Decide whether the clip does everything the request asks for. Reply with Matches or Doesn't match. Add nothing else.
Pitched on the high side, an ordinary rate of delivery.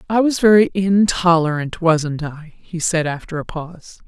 Doesn't match